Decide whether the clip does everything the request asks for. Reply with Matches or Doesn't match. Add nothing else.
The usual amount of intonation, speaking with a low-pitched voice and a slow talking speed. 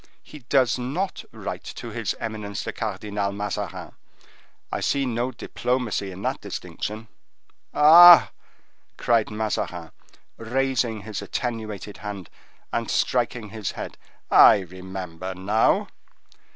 Matches